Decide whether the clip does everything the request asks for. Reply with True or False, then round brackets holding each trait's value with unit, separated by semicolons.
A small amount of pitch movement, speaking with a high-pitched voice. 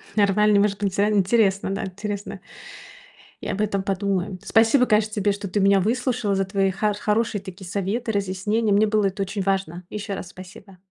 True (1.6 semitones; 200 Hz)